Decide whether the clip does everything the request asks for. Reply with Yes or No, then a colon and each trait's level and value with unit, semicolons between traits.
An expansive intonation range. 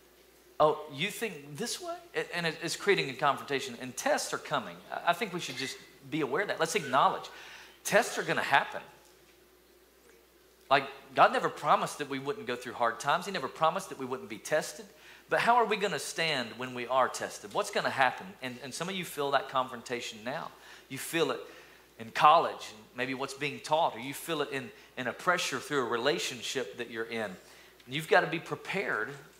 Yes: wide, 8.0 semitones